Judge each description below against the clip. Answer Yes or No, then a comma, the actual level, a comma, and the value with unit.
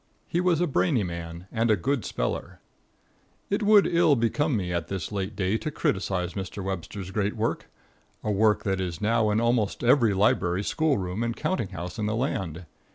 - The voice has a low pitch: Yes, low, 105 Hz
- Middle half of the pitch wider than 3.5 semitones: Yes, average, 4.6 semitones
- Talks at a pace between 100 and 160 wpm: No, average, 190 wpm